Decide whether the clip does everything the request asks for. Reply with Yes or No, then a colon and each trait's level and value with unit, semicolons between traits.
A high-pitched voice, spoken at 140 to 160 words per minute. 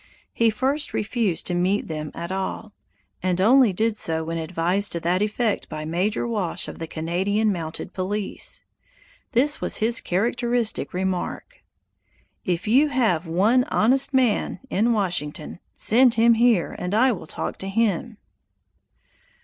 Yes: high, 205 Hz; average, 145 wpm